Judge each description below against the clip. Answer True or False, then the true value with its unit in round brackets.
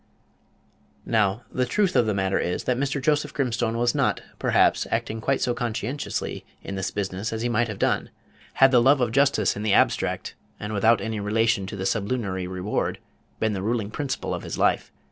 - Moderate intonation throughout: True (3.6 semitones)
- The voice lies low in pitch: True (115 Hz)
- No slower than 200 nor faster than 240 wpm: False (190 wpm)